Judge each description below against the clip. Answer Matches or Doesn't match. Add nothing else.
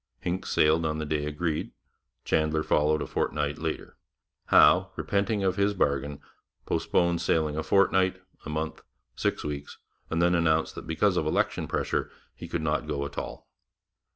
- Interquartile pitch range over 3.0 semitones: Doesn't match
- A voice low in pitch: Matches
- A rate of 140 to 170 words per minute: Matches